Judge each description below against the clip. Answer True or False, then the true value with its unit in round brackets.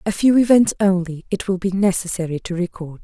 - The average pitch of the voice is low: False (190 Hz)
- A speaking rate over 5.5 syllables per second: True (5.7 syllables/s)